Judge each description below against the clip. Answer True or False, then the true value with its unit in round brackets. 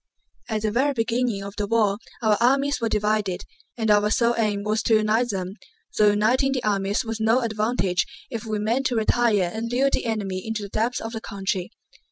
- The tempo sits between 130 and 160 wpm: False (205 wpm)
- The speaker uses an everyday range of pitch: False (2.3 semitones)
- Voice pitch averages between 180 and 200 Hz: False (220 Hz)